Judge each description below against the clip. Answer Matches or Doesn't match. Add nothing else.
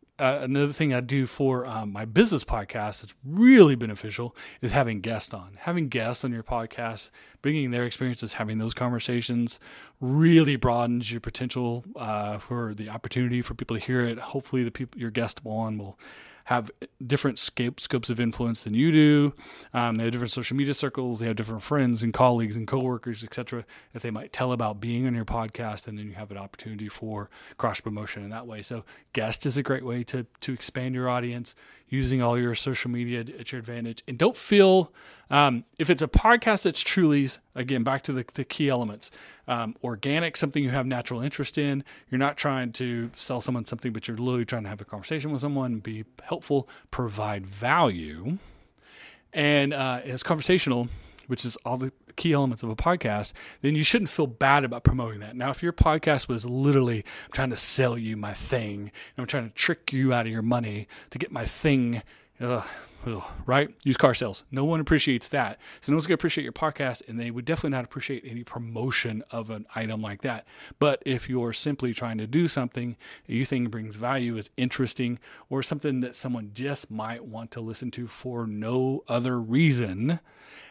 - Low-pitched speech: Matches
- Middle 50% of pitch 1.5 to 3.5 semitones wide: Matches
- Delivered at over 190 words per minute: Matches